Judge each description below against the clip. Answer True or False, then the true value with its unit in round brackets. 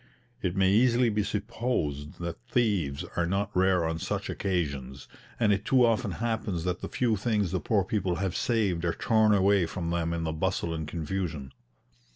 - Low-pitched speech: True (95 Hz)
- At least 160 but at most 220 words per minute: True (185 wpm)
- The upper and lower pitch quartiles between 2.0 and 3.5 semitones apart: False (4.2 semitones)